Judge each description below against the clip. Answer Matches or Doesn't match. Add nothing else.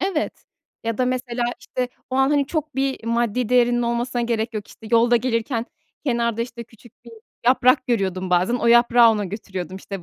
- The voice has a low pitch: Doesn't match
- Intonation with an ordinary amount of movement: Doesn't match